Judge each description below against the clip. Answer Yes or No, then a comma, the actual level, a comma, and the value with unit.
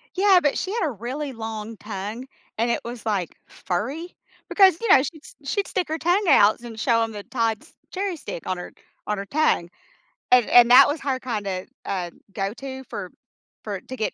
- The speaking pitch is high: Yes, high, 240 Hz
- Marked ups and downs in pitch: Yes, wide, 6.2 semitones